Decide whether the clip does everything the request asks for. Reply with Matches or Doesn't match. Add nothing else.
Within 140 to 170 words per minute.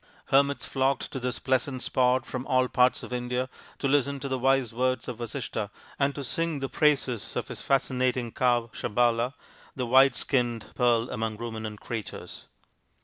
Matches